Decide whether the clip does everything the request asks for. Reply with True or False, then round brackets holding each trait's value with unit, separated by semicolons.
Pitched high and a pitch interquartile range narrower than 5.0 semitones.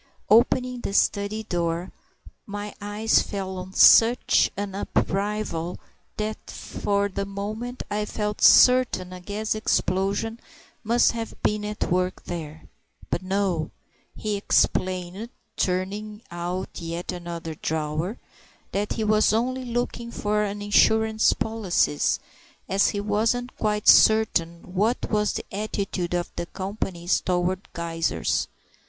True (200 Hz; 3.1 semitones)